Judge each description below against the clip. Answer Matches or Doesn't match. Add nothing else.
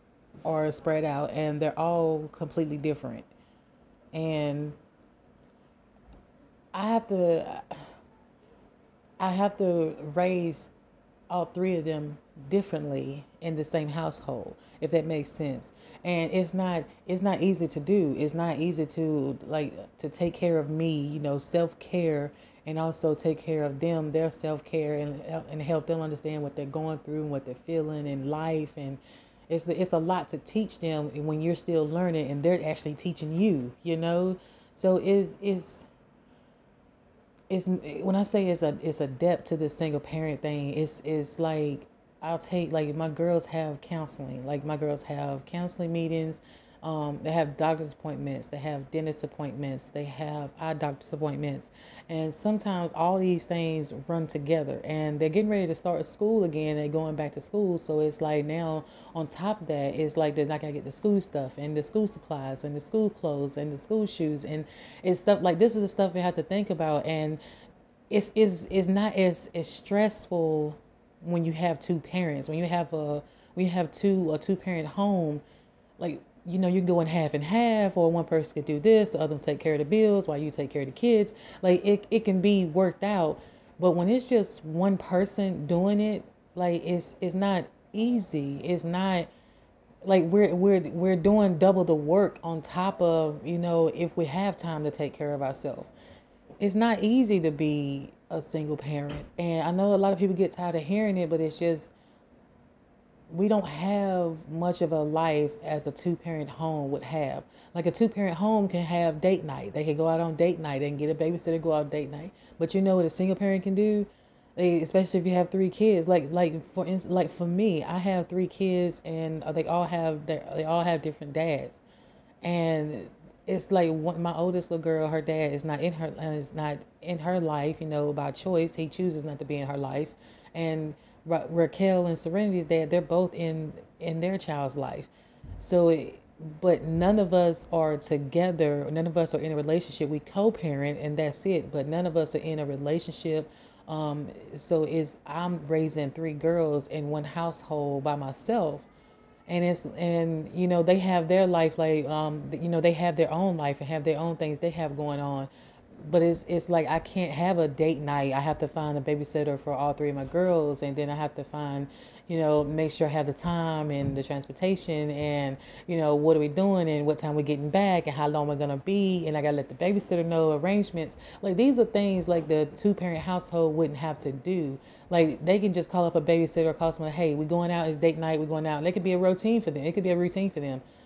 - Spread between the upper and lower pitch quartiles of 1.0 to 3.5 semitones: Matches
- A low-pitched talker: Doesn't match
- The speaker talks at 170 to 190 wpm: Doesn't match